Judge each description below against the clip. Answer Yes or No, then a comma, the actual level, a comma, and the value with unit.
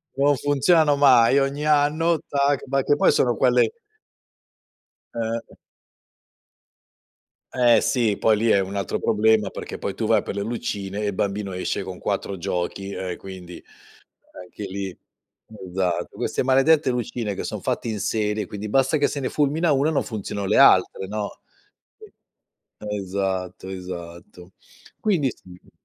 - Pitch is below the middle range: Yes, low, 110 Hz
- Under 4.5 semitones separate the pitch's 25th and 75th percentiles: No, wide, 6.2 semitones